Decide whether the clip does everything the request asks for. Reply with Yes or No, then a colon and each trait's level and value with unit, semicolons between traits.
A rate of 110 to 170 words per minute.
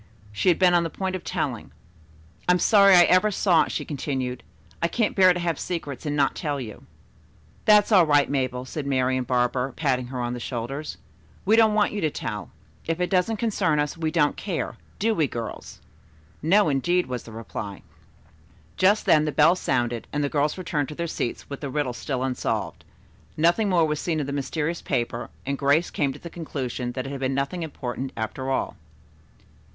No: average, 200 wpm